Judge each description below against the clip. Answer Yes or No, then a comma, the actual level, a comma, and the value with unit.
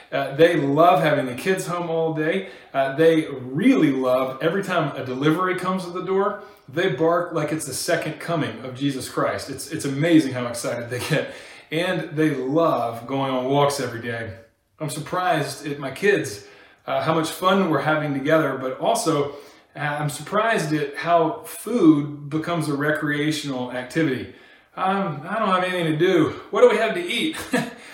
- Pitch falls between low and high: Yes, medium, 155 Hz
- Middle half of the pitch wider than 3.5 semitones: Yes, average, 4.1 semitones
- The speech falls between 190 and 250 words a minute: No, average, 180 wpm